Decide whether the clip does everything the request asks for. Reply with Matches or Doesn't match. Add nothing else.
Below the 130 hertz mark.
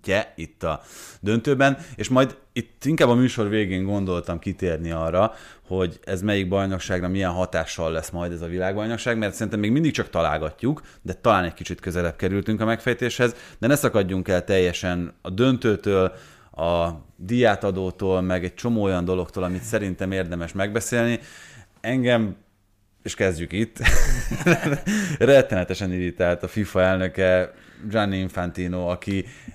Matches